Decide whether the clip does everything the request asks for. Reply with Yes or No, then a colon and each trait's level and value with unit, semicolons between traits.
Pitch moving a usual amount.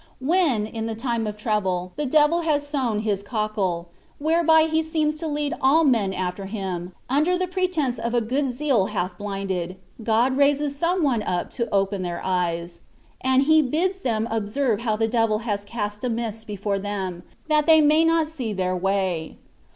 No: wide, 6.8 semitones